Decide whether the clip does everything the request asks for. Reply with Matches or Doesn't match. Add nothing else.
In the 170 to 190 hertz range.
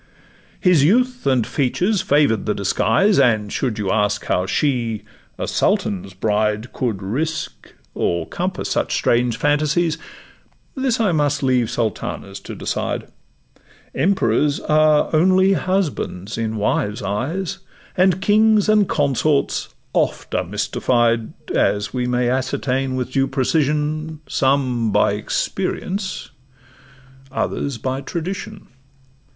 Doesn't match